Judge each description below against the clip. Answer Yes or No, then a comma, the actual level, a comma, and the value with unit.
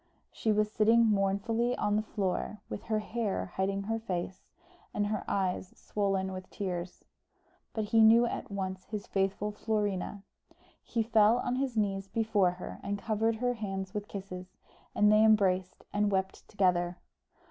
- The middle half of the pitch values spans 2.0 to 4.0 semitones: Yes, narrow, 2.4 semitones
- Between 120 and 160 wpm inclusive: Yes, average, 155 wpm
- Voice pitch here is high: Yes, high, 205 Hz